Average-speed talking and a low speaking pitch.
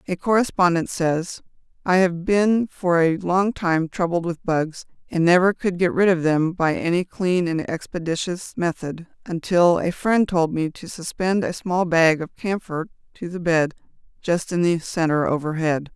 No: average, 175 wpm; medium, 175 Hz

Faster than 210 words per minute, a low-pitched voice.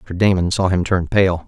Yes: fast, 245 wpm; very low, 90 Hz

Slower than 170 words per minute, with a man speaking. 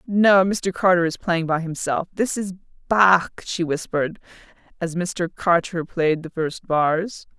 No: average, 145 wpm; female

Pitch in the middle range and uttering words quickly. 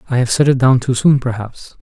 No: low, 125 Hz; fast, 265 wpm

